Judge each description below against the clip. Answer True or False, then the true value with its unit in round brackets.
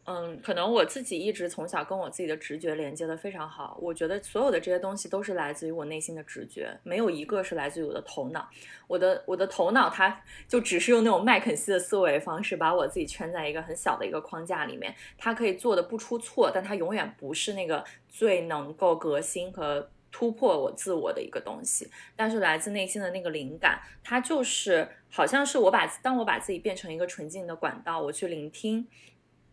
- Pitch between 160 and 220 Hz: True (185 Hz)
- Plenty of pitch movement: True (5.7 semitones)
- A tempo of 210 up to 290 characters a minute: False (330 characters per minute)